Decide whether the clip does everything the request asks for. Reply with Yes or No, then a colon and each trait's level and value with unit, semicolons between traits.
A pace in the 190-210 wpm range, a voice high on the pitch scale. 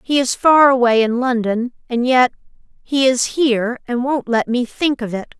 Yes: average, 200 wpm; very high, 250 Hz